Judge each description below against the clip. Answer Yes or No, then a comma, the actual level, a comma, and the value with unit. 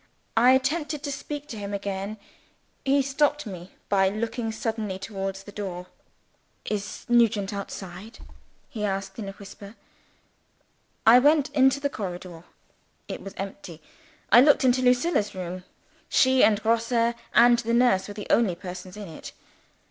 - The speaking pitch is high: Yes, high, 215 Hz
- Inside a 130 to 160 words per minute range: Yes, average, 150 wpm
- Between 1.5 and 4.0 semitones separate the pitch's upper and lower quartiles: No, average, 4.4 semitones